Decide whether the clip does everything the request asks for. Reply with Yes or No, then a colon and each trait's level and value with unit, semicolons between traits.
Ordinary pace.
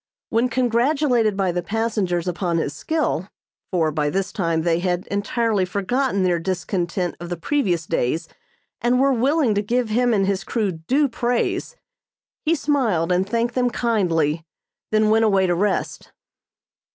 Yes: average, 155 wpm